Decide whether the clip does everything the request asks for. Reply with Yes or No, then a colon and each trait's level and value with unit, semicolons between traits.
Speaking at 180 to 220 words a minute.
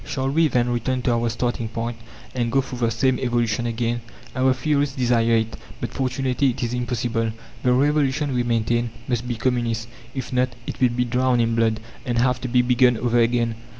Yes: average, 200 wpm